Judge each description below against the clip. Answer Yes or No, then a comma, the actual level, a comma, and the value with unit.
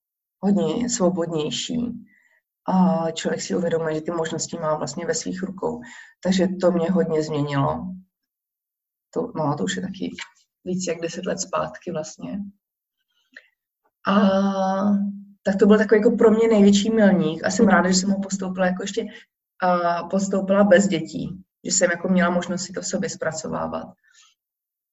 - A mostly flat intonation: No, average, 3.2 semitones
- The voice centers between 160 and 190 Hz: Yes, medium, 185 Hz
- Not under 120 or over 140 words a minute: No, average, 155 wpm